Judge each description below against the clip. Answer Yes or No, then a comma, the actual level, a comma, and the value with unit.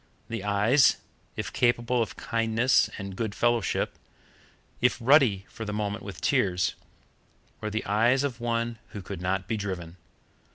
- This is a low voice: Yes, low, 110 Hz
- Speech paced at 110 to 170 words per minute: Yes, average, 140 wpm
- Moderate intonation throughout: Yes, average, 3.1 semitones